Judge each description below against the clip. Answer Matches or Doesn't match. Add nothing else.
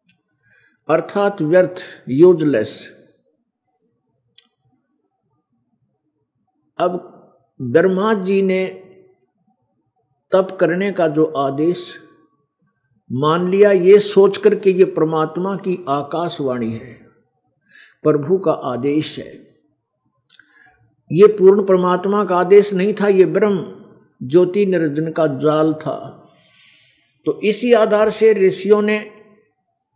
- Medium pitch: Matches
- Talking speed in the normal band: Doesn't match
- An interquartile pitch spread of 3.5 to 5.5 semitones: Matches